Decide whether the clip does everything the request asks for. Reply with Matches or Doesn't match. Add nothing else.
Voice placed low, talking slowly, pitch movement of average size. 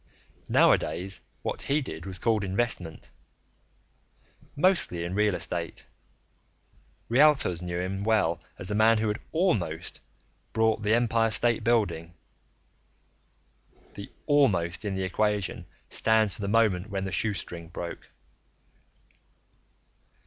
Matches